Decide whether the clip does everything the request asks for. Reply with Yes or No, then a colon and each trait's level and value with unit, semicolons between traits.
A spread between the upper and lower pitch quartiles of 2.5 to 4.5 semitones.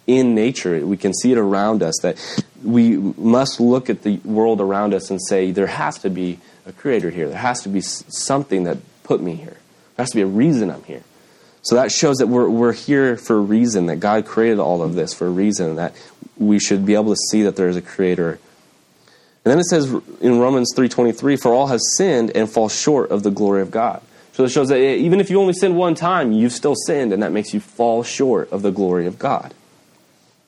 Yes: average, 3.8 semitones